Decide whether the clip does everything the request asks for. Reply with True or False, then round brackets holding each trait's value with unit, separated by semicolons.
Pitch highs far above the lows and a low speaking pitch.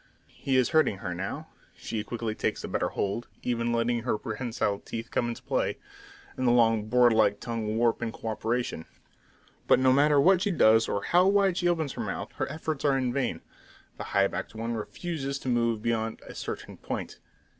False (3.6 semitones; 120 Hz)